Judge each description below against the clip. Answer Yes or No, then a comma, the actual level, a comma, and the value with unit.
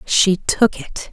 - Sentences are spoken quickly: No, average, 160 wpm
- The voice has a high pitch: Yes, high, 200 Hz